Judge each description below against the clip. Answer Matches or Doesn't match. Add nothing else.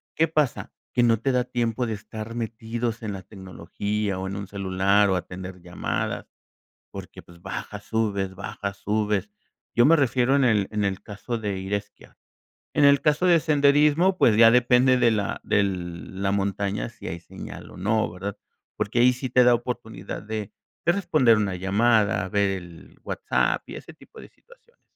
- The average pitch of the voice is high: Doesn't match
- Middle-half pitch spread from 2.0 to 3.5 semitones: Doesn't match